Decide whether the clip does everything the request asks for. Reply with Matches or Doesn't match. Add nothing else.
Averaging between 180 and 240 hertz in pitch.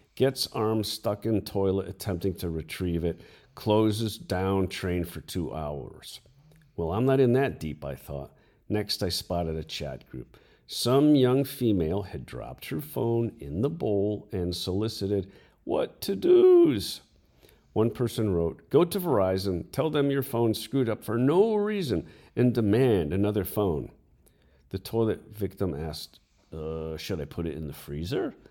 Doesn't match